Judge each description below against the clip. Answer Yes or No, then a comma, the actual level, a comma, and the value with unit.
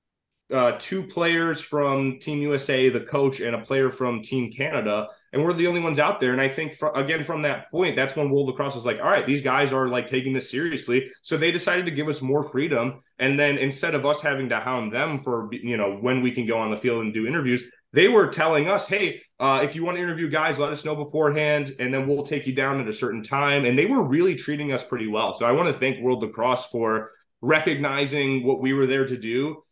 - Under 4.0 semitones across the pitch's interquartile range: Yes, average, 2.9 semitones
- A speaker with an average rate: No, fast, 250 wpm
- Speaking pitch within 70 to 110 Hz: No, low, 135 Hz